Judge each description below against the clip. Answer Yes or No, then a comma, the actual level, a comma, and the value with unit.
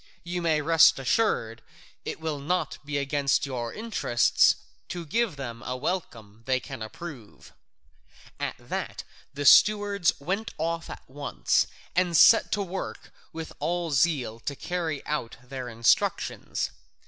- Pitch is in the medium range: Yes, medium, 150 Hz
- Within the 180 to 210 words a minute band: No, slow, 135 wpm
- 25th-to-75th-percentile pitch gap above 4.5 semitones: Yes, average, 5.3 semitones